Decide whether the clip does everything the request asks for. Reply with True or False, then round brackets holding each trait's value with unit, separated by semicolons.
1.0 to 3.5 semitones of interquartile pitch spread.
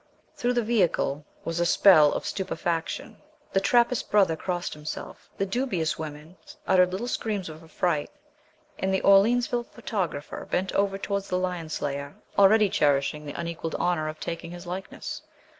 False (4.0 semitones)